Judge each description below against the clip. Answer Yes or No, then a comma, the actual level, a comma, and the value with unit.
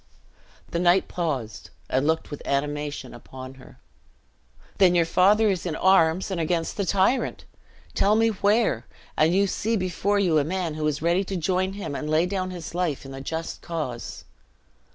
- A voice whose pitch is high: No, medium, 170 Hz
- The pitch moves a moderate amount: Yes, average, 3.9 semitones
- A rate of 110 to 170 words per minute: No, average, 180 wpm